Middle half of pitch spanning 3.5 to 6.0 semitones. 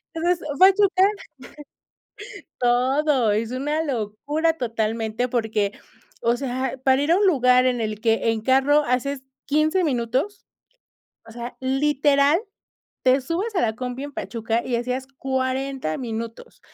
Yes: average, 3.8 semitones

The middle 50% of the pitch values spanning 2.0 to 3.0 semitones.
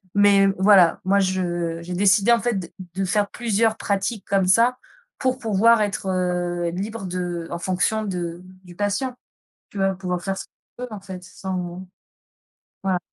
Yes: narrow, 2.6 semitones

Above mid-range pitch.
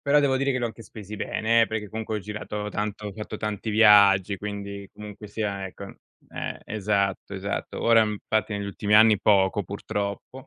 No: low, 105 Hz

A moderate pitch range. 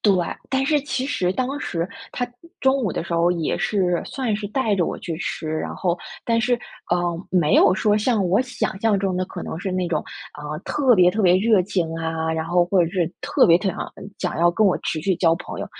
Yes: average, 4.1 semitones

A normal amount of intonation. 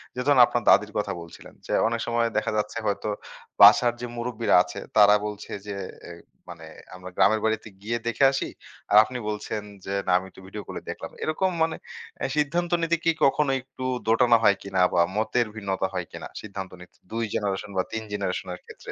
Yes: average, 3.5 semitones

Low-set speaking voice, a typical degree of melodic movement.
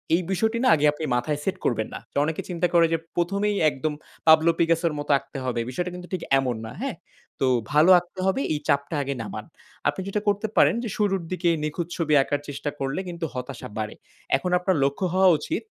No: medium, 165 Hz; average, 4.7 semitones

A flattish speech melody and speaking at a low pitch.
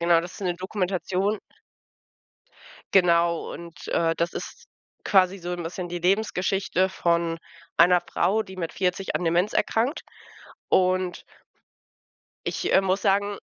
No: narrow, 2.0 semitones; medium, 180 Hz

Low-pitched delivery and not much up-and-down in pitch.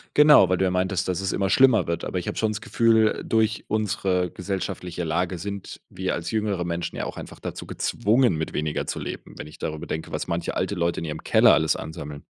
No: very low, 90 Hz; average, 4.0 semitones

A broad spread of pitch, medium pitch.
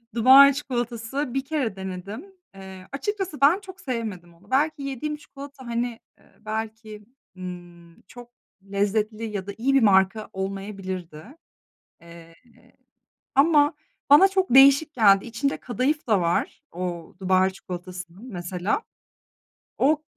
No: wide, 6.6 semitones; high, 225 Hz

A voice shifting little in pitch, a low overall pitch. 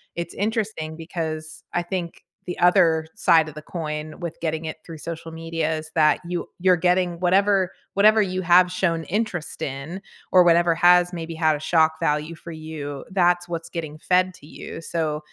No: narrow, 2.2 semitones; medium, 170 Hz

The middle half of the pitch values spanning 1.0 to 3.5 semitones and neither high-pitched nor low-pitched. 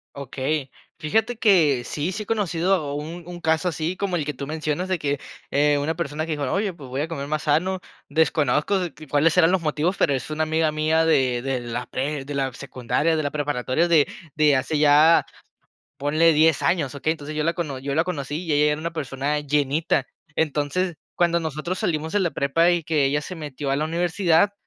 Yes: average, 2.8 semitones; medium, 155 Hz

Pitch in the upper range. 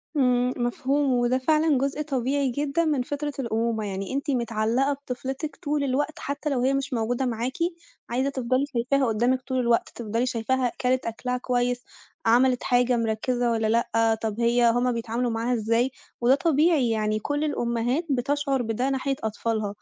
Yes: very high, 250 Hz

